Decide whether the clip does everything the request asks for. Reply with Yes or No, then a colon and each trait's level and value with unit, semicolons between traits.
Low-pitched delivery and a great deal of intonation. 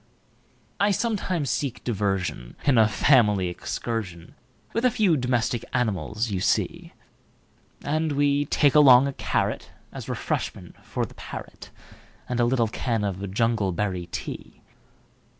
Yes: low, 120 Hz; wide, 5.8 semitones